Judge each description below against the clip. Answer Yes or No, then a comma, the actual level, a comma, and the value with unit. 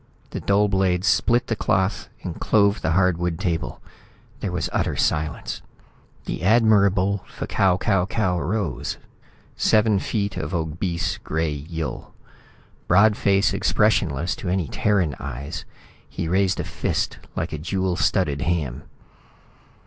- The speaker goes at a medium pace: No, slow, 130 wpm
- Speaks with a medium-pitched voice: No, very low, 90 Hz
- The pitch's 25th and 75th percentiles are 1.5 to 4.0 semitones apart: Yes, average, 3.6 semitones